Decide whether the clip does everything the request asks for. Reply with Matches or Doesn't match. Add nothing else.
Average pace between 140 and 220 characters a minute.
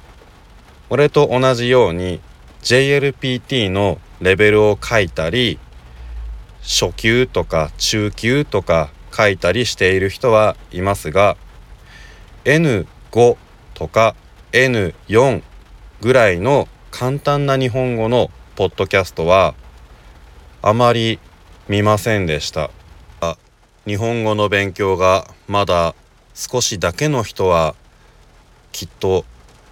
Matches